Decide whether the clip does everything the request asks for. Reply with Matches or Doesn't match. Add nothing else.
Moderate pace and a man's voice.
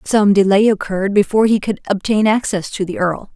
Doesn't match